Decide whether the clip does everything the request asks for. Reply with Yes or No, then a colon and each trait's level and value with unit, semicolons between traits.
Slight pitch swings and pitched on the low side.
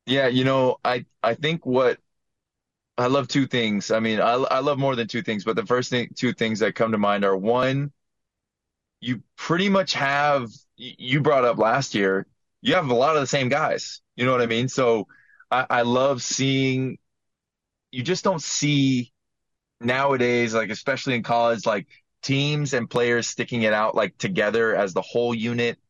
No: average, 3.0 semitones; low, 125 Hz